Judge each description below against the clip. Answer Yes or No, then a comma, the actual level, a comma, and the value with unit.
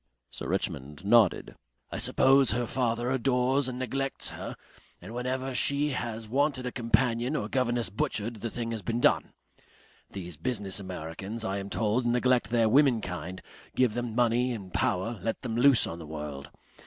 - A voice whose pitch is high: No, low, 115 Hz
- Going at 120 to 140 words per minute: No, average, 165 wpm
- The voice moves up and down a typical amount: Yes, average, 4.1 semitones